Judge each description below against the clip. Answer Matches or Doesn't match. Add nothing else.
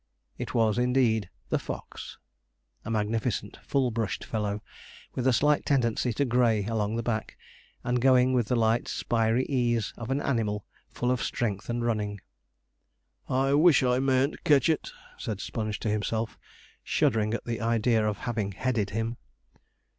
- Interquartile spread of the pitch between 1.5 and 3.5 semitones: Matches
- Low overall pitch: Matches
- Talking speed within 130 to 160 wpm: Matches